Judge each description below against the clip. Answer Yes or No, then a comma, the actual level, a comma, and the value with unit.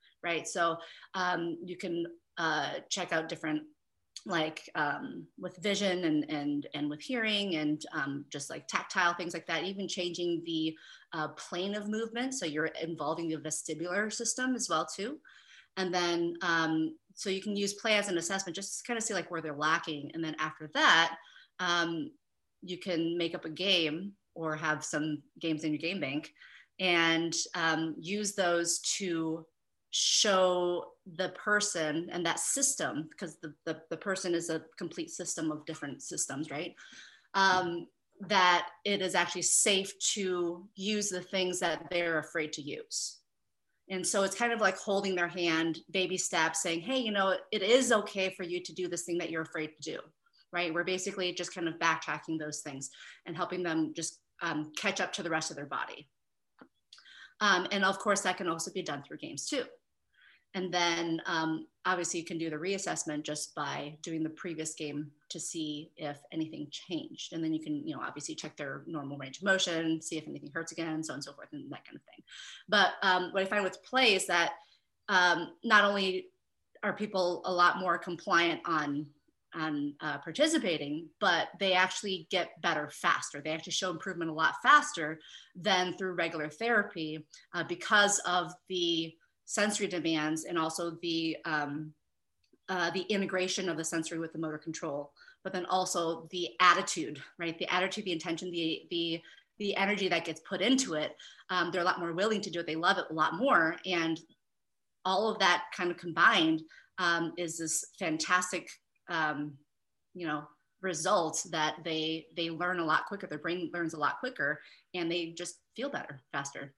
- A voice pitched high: No, medium, 170 Hz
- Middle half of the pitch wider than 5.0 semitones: No, average, 2.9 semitones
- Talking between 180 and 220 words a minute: Yes, average, 185 wpm